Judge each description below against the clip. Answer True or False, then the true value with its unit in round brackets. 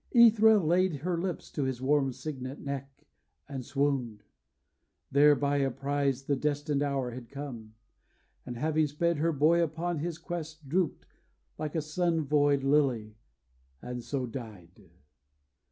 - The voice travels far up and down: False (3.1 semitones)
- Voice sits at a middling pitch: True (145 Hz)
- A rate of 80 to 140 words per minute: True (135 wpm)